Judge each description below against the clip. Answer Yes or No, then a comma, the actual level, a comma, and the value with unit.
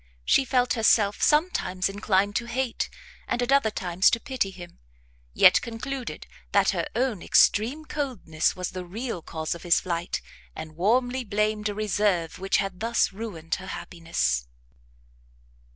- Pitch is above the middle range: Yes, high, 205 Hz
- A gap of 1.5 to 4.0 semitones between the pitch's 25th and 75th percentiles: No, average, 5.3 semitones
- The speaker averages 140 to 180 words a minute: Yes, average, 150 wpm